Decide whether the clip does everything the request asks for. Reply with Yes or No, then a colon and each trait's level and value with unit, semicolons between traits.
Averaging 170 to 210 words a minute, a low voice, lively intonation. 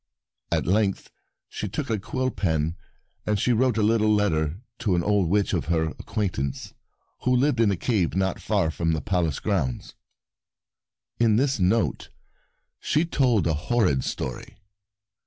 No: average, 155 wpm; low, 100 Hz; wide, 5.7 semitones